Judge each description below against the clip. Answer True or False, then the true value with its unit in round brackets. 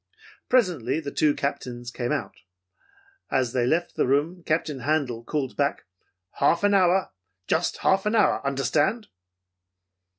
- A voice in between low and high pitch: True (145 Hz)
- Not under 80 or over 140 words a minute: True (135 wpm)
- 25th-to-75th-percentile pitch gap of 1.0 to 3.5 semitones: False (5.2 semitones)